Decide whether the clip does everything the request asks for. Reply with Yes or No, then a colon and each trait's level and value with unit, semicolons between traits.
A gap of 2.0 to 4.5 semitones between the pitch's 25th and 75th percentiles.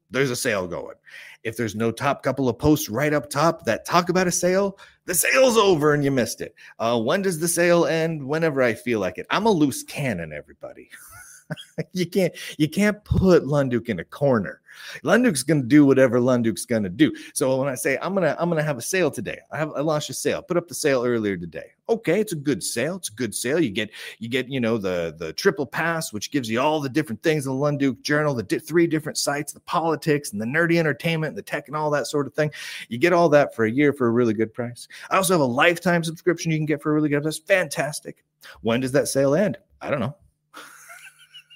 No: average, 5.0 semitones